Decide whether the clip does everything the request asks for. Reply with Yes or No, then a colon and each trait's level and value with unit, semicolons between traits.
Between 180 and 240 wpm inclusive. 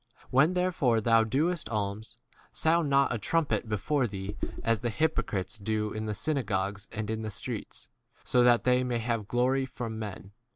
No: average, 170 wpm